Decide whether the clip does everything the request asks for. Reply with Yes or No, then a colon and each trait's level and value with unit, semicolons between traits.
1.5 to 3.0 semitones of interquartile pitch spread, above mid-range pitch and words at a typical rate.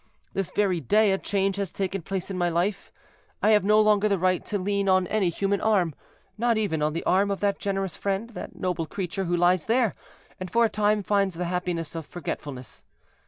No: narrow, 2.6 semitones; high, 195 Hz; fast, 210 wpm